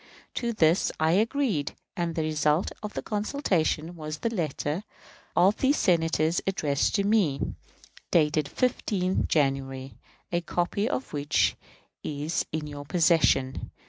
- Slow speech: Yes, slow, 130 wpm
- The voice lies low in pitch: No, medium, 165 Hz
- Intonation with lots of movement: No, average, 4.8 semitones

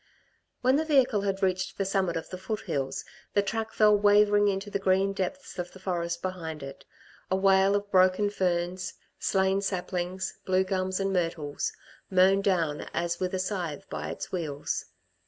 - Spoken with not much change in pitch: Yes, narrow, 2.1 semitones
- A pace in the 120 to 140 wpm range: No, average, 170 wpm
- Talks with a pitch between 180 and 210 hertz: Yes, high, 190 Hz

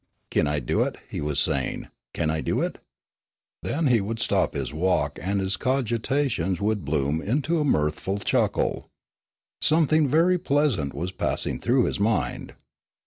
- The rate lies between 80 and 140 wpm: No, average, 155 wpm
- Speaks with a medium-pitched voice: No, low, 100 Hz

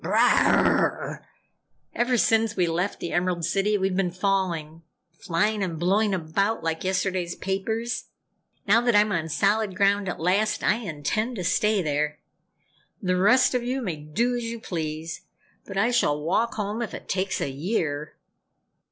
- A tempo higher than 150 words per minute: Yes, average, 160 wpm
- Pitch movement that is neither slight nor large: Yes, average, 4.4 semitones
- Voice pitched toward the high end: Yes, high, 195 Hz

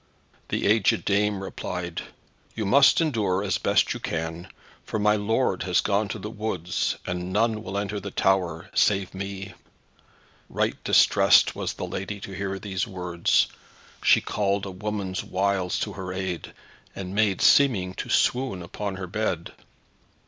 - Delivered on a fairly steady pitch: Yes, narrow, 2.3 semitones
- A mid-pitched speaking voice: No, very low, 95 Hz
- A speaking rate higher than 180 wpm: No, average, 155 wpm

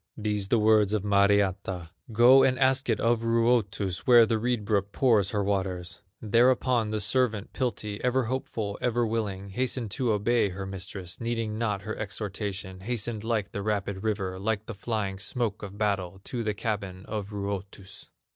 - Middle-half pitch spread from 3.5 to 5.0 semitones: No, average, 2.7 semitones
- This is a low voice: Yes, low, 105 Hz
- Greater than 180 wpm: No, average, 165 wpm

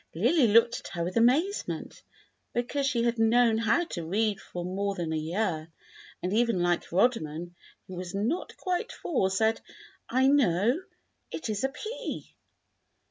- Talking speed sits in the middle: Yes, average, 155 wpm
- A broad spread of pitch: Yes, wide, 5.9 semitones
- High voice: Yes, high, 220 Hz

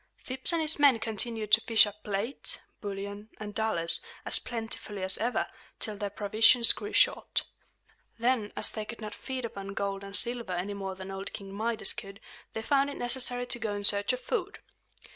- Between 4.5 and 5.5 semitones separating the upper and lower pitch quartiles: No, average, 3.3 semitones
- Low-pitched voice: No, high, 220 Hz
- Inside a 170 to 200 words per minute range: Yes, average, 190 wpm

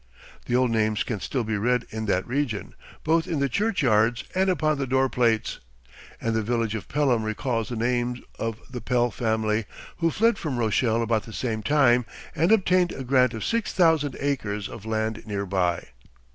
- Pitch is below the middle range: Yes, low, 120 Hz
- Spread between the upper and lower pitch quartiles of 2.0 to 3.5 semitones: No, average, 4.2 semitones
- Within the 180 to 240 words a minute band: Yes, average, 185 wpm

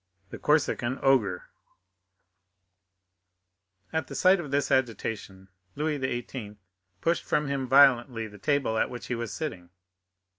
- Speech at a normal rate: No, slow, 125 wpm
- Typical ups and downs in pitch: Yes, average, 4.2 semitones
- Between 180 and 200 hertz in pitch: No, low, 130 Hz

